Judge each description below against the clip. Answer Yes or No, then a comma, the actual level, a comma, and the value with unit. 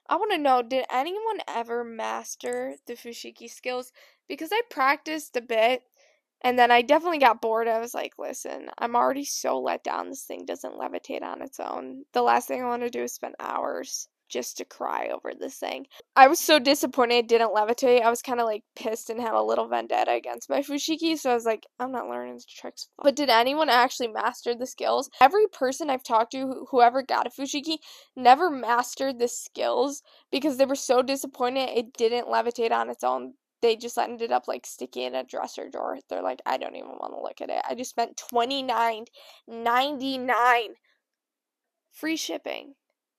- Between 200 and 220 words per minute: Yes, fast, 205 wpm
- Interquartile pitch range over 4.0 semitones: No, average, 3.4 semitones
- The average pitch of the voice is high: Yes, very high, 250 Hz